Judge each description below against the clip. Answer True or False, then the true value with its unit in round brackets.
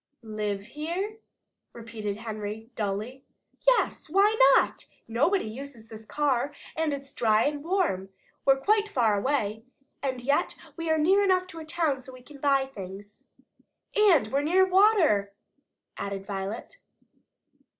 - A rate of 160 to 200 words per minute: False (145 wpm)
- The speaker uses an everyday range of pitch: False (7.3 semitones)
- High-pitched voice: True (270 Hz)